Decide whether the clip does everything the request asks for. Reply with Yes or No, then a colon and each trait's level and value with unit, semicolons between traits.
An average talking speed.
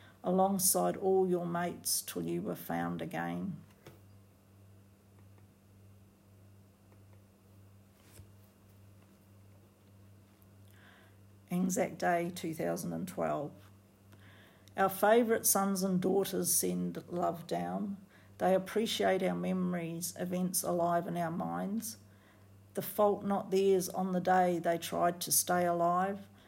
No: slow, 100 wpm